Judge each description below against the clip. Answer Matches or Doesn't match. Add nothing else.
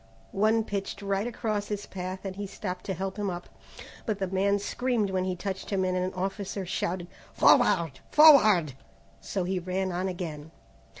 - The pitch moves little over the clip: Matches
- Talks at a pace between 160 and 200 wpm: Matches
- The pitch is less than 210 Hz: Matches